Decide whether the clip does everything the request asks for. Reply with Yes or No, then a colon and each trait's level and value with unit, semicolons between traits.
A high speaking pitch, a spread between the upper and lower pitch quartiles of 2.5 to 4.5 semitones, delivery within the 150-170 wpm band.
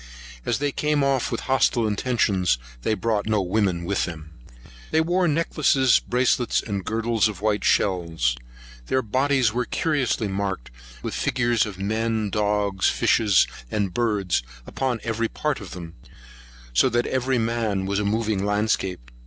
No: low, 110 Hz; average, 4.1 semitones; average, 155 wpm